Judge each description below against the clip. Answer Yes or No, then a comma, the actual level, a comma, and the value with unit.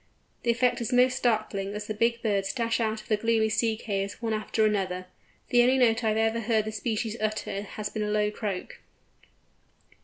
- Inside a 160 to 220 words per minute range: Yes, fast, 205 wpm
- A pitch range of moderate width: No, narrow, 1.8 semitones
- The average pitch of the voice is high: Yes, high, 220 Hz